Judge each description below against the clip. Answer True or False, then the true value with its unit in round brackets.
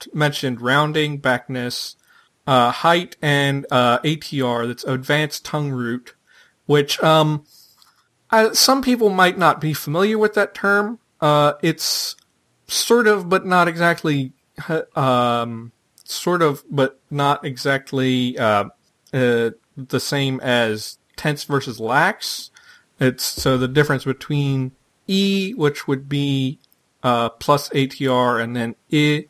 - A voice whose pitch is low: False (145 Hz)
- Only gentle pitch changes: False (3.6 semitones)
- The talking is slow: True (125 wpm)